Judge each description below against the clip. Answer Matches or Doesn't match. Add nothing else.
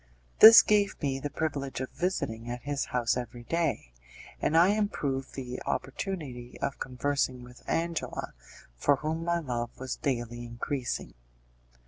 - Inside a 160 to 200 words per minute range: Doesn't match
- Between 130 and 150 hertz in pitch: Matches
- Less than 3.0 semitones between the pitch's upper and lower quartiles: Doesn't match